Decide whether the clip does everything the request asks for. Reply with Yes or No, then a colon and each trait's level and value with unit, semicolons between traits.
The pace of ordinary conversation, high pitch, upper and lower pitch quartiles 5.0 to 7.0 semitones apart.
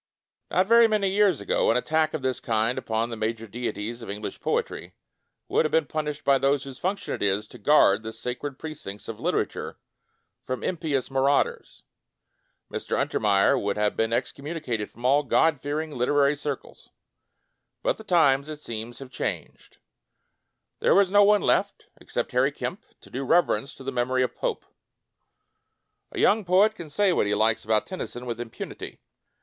No: average, 180 wpm; low, 135 Hz; wide, 5.6 semitones